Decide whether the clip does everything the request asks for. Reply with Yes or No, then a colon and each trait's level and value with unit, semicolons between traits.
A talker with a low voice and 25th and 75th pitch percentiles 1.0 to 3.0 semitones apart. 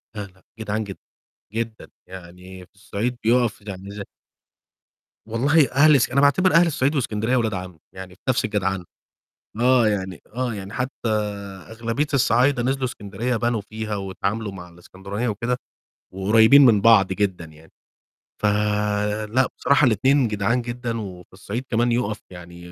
No: low, 110 Hz; average, 4.0 semitones